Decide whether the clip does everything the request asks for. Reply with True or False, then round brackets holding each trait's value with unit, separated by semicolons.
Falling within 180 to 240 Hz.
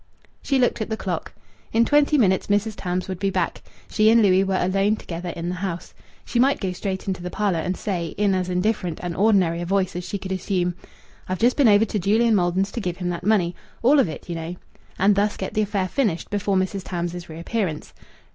True (190 Hz)